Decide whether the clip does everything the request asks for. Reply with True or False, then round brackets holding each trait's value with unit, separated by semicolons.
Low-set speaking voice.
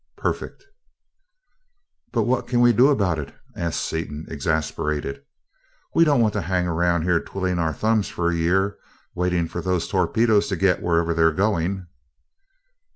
True (90 Hz)